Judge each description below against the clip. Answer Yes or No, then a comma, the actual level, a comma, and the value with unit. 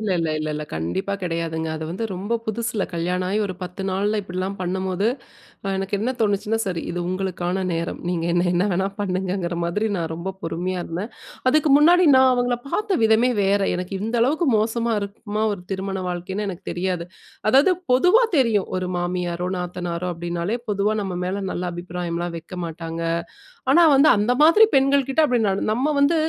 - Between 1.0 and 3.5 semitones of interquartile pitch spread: No, average, 4.3 semitones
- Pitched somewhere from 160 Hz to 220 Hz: Yes, high, 190 Hz